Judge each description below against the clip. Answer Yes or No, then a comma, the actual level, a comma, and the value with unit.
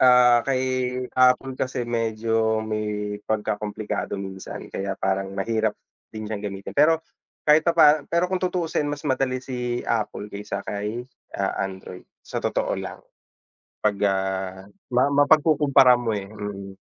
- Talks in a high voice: No, low, 115 Hz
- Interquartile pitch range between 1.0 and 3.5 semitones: No, average, 4.3 semitones